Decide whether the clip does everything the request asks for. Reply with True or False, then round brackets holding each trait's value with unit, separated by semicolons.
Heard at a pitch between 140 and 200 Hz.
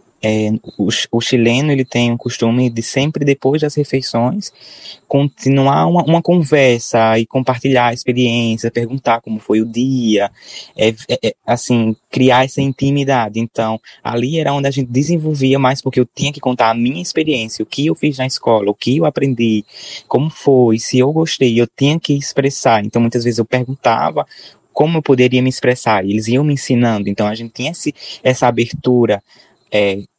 False (125 Hz)